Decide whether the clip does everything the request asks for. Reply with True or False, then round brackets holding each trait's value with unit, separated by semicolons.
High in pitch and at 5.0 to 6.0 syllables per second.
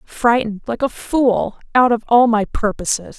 False (230 Hz; 4.6 syllables/s)